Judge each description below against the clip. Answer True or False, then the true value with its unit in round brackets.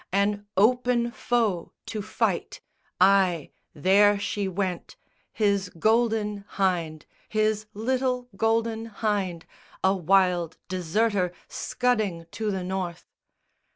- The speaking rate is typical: False (100 wpm)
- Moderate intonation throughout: True (3.2 semitones)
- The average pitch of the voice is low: False (205 Hz)